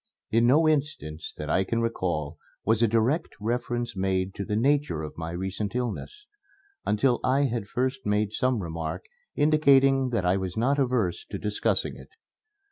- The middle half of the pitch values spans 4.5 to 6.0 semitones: Yes, wide, 5.6 semitones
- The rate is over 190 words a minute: No, average, 165 wpm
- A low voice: Yes, low, 115 Hz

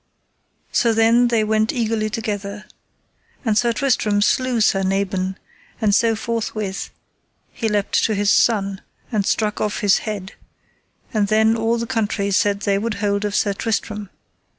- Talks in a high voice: Yes, high, 215 Hz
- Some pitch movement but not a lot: No, narrow, 1.9 semitones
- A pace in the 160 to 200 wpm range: No, average, 150 wpm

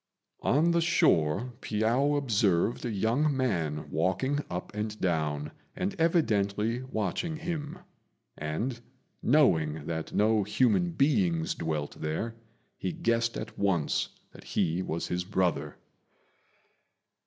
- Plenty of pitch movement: Yes, wide, 8.4 semitones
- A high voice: No, low, 105 Hz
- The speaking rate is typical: No, slow, 115 wpm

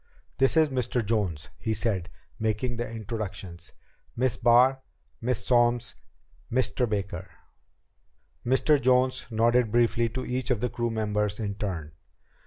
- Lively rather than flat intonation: No, average, 3.2 semitones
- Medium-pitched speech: No, low, 115 Hz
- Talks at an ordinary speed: No, slow, 130 wpm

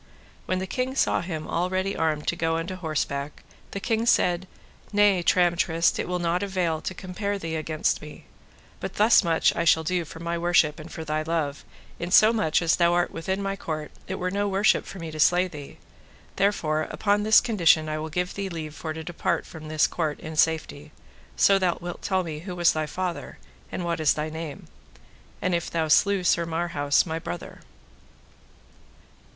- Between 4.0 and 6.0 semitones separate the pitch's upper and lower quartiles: No, average, 3.0 semitones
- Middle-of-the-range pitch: Yes, medium, 170 Hz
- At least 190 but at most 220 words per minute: Yes, average, 195 wpm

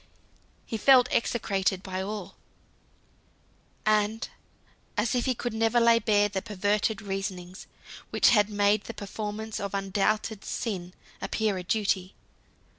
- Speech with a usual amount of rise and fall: No, narrow, 2.1 semitones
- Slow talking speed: Yes, slow, 125 wpm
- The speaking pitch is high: Yes, high, 210 Hz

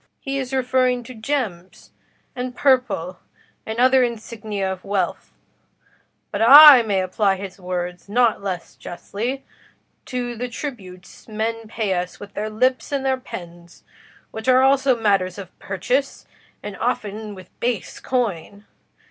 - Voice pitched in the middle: No, high, 220 Hz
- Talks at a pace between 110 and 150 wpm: Yes, average, 140 wpm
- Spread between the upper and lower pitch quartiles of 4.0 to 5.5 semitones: Yes, average, 4.7 semitones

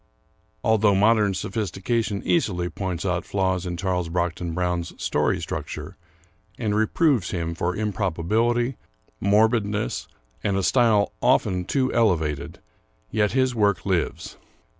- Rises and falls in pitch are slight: No, average, 3.8 semitones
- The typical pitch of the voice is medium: No, low, 100 Hz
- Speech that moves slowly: Yes, slow, 120 wpm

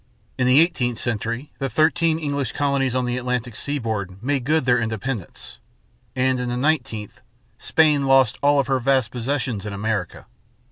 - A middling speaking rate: Yes, average, 160 wpm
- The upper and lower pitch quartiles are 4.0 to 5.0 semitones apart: No, average, 3.5 semitones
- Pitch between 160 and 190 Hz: No, low, 130 Hz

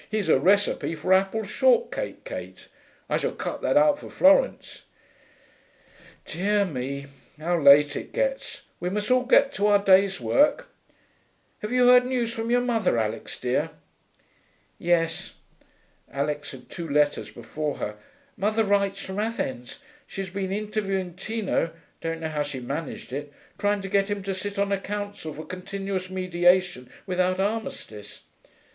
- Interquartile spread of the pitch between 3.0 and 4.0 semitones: No, average, 4.8 semitones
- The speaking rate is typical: Yes, average, 150 wpm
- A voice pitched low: No, high, 195 Hz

